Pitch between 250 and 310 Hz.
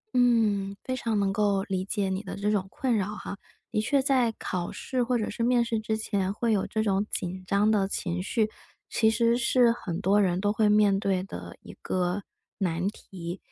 No: high, 205 Hz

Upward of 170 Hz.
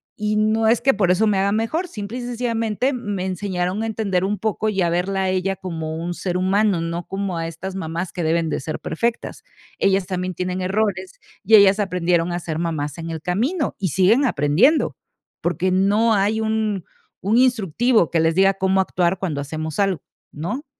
Yes: high, 190 Hz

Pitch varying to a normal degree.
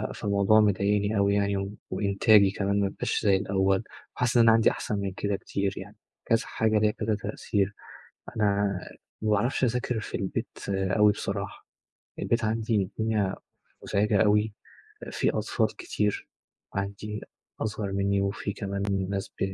No: narrow, 1.6 semitones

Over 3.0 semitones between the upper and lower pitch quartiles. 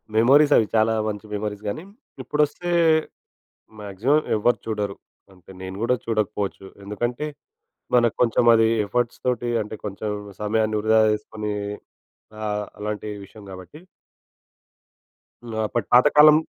No: average, 2.7 semitones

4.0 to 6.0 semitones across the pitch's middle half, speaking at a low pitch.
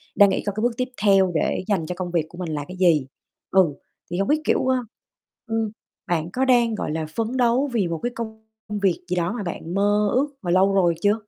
No: average, 4.4 semitones; high, 195 Hz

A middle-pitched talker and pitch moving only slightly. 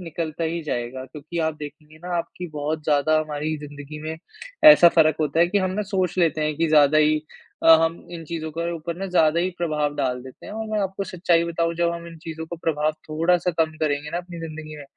Yes: medium, 160 Hz; narrow, 2.0 semitones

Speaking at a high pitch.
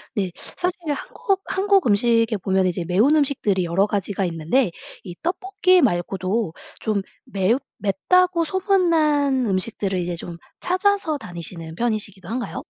Yes: high, 220 Hz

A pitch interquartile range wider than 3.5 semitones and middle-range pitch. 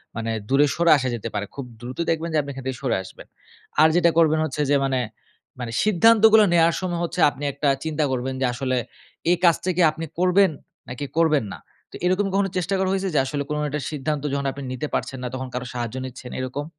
Yes: average, 4.7 semitones; medium, 150 Hz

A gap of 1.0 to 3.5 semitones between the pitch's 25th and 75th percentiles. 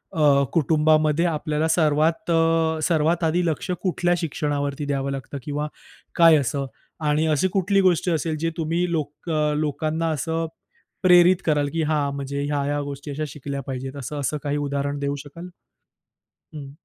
Yes: narrow, 2.4 semitones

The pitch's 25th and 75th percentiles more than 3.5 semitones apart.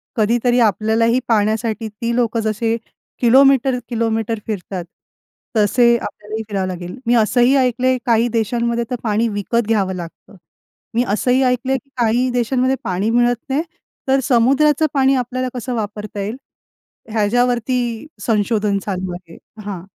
No: average, 2.8 semitones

